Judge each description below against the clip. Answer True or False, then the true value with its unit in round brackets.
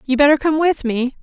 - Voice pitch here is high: True (280 Hz)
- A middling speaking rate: False (245 wpm)